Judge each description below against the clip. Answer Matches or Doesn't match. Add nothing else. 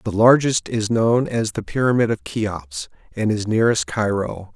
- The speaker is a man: Matches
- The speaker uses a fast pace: Doesn't match